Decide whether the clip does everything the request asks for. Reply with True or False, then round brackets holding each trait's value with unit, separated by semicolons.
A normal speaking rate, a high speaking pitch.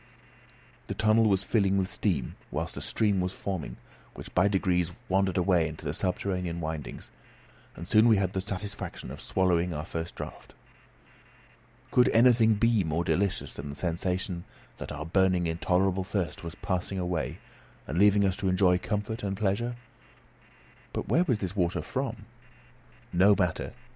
False (155 wpm; 95 Hz)